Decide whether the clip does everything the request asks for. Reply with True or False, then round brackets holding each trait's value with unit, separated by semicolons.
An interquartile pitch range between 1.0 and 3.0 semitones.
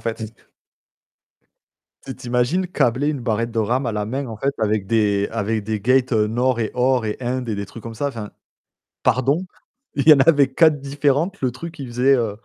False (3.7 semitones)